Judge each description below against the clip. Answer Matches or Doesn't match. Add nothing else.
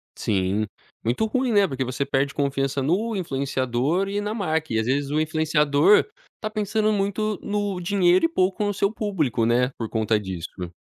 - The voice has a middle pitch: Matches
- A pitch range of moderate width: Doesn't match